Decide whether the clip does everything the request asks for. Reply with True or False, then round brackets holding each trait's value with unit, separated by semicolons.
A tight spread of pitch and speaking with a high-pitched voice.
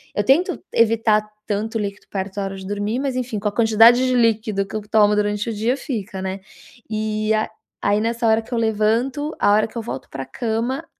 True (2.1 semitones; 220 Hz)